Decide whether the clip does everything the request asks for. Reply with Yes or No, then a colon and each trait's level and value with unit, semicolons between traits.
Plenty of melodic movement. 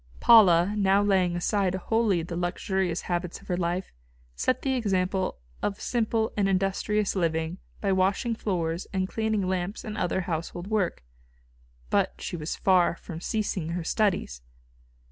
No: average, 2.9 semitones